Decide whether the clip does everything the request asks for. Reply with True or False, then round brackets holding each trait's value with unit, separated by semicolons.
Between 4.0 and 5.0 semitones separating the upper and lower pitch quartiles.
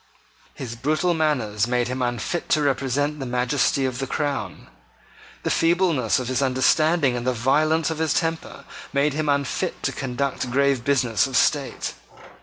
False (3.4 semitones)